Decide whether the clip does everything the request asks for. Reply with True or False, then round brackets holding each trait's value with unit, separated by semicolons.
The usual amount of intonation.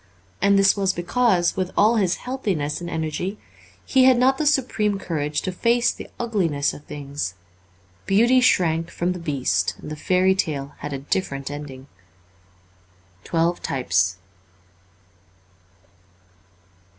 False (6.0 semitones)